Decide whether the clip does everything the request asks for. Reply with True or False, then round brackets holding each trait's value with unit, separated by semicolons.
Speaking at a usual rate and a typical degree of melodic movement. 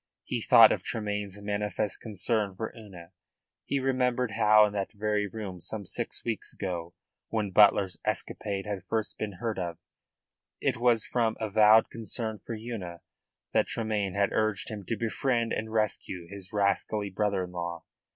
False (160 wpm; 2.3 semitones)